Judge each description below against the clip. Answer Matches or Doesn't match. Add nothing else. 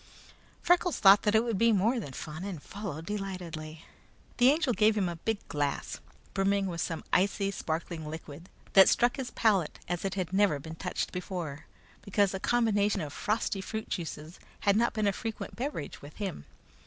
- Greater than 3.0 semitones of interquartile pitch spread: Matches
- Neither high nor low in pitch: Doesn't match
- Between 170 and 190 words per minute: Matches